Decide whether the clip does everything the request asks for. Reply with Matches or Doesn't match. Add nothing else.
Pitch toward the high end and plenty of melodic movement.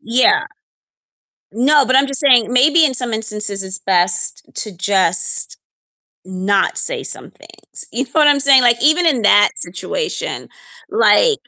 Matches